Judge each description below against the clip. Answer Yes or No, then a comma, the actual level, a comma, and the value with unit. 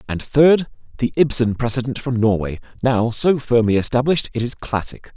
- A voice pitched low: Yes, low, 125 Hz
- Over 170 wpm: No, average, 165 wpm